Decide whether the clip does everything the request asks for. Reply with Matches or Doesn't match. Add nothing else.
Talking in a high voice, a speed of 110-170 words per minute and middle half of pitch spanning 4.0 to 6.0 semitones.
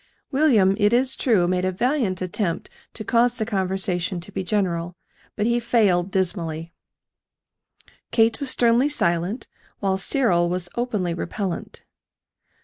Matches